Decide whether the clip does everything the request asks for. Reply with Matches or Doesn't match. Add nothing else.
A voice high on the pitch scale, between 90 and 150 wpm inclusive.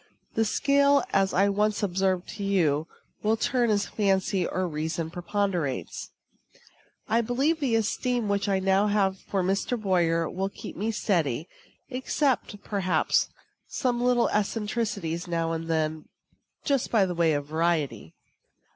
Matches